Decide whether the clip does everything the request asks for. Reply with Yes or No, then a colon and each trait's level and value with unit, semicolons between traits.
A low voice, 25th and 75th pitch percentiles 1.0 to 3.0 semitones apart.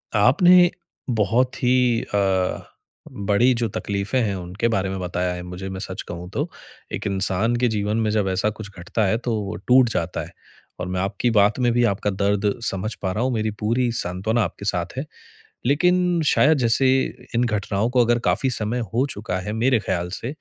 No: low, 105 Hz; average, 4.1 semitones